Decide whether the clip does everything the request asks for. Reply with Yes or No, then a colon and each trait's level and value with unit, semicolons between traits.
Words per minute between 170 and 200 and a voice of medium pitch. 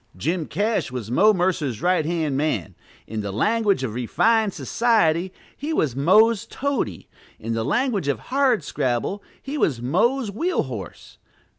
No: average, 145 wpm; medium, 170 Hz